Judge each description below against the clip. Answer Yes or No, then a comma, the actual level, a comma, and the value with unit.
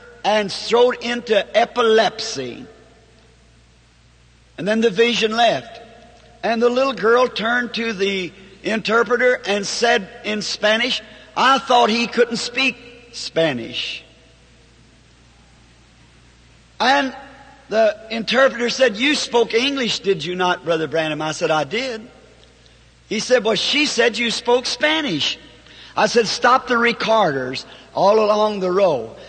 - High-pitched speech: Yes, high, 230 Hz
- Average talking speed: No, slow, 125 wpm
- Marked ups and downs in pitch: No, average, 4.1 semitones